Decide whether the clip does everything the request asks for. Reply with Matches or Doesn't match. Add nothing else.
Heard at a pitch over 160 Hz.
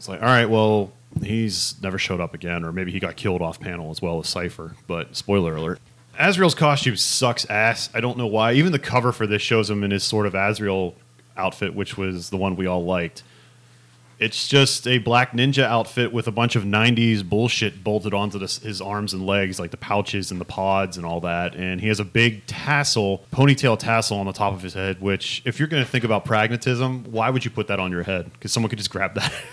Doesn't match